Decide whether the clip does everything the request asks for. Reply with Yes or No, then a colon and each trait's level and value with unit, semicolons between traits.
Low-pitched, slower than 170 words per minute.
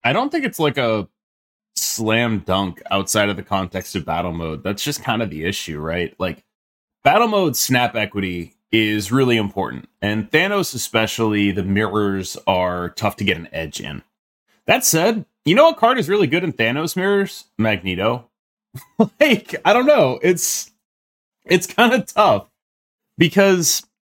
Yes: low, 115 Hz; average, 160 wpm